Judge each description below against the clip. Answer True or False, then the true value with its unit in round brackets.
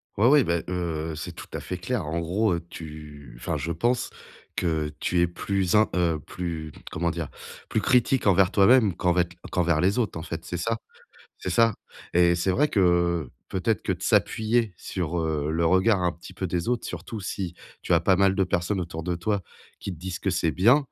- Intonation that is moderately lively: True (3.0 semitones)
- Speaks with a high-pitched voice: False (90 Hz)